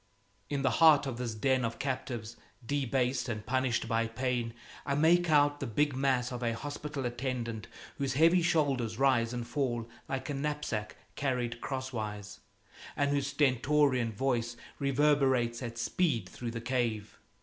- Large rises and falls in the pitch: No, average, 3.3 semitones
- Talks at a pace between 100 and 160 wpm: Yes, average, 150 wpm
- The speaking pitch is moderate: No, low, 130 Hz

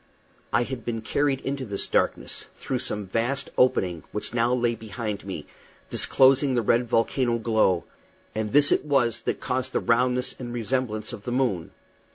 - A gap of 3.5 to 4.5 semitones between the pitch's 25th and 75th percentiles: No, average, 3.1 semitones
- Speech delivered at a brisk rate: No, average, 170 wpm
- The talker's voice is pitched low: Yes, low, 120 Hz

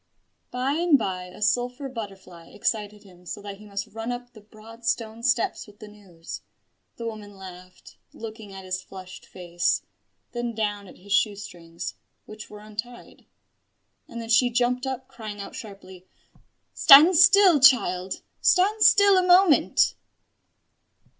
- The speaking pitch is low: No, high, 215 Hz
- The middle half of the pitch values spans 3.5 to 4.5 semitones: Yes, average, 4.2 semitones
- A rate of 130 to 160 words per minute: Yes, average, 150 wpm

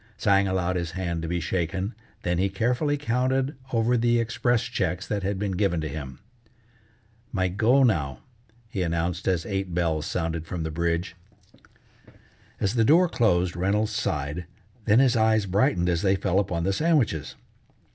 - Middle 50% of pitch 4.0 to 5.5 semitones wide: Yes, average, 4.7 semitones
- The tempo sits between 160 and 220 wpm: Yes, average, 165 wpm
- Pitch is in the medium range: No, very low, 95 Hz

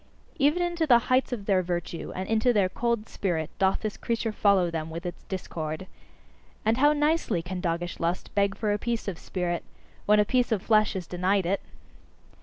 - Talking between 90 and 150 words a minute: No, average, 195 wpm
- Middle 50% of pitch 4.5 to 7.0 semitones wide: Yes, average, 4.8 semitones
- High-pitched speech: Yes, high, 200 Hz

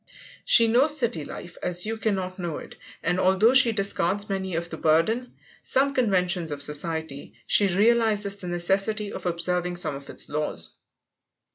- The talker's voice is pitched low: No, medium, 185 Hz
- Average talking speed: Yes, average, 160 wpm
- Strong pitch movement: No, average, 4.3 semitones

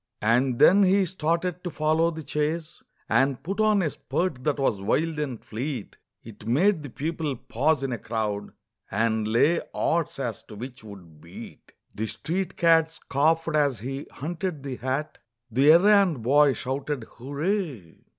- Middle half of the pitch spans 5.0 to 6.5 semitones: Yes, wide, 5.4 semitones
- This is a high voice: No, medium, 145 Hz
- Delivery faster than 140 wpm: Yes, average, 160 wpm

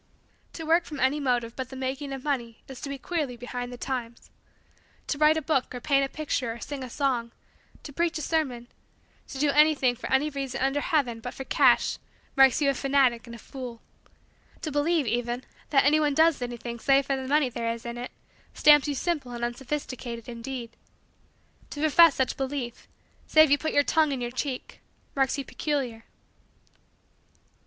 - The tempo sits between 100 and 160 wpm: No, average, 190 wpm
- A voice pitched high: Yes, very high, 270 Hz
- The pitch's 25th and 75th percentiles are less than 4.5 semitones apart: Yes, average, 3.2 semitones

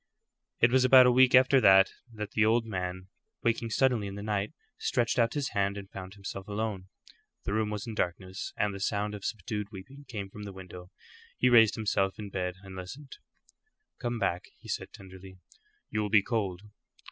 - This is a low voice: Yes, low, 105 Hz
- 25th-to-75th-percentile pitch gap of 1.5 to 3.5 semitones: Yes, average, 3.1 semitones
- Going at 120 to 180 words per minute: No, average, 190 wpm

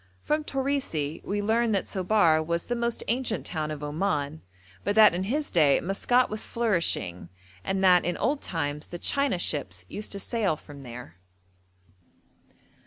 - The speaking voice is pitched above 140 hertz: Yes, medium, 185 Hz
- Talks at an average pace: Yes, average, 160 wpm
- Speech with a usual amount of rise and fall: No, wide, 7.0 semitones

